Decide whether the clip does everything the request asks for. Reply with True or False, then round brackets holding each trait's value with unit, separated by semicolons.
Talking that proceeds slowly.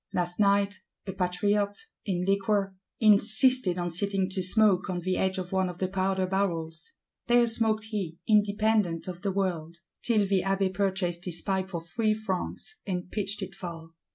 False (165 wpm)